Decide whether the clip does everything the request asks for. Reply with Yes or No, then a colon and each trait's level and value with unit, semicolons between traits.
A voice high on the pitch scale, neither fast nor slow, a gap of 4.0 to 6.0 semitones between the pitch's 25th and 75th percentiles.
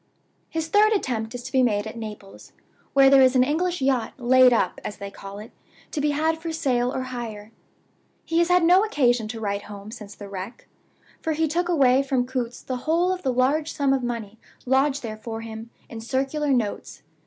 No: very high, 255 Hz; fast, 210 wpm; average, 5.0 semitones